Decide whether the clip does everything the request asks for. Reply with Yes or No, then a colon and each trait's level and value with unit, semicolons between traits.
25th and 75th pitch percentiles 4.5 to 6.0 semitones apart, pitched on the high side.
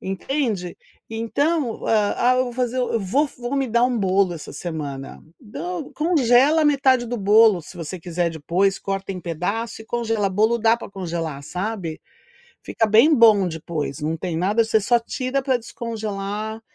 Yes: average, 5.1 semitones; high, 215 Hz